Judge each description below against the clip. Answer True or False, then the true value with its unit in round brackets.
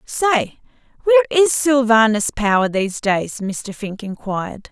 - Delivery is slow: True (125 wpm)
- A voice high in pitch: True (230 Hz)